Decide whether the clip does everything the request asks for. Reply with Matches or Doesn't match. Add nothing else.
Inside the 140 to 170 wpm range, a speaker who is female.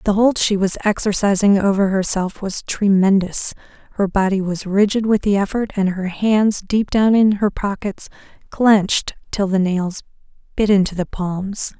Matches